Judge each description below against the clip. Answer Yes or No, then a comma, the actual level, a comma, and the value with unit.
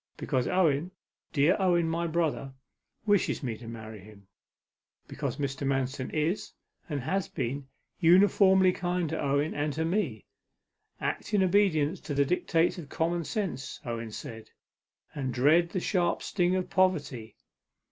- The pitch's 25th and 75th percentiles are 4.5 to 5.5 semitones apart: Yes, average, 5.1 semitones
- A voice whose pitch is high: No, medium, 160 Hz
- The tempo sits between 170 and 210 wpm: No, average, 145 wpm